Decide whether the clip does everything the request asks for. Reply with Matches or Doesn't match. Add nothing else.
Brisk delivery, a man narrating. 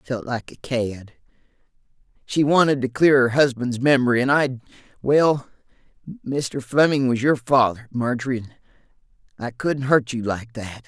Doesn't match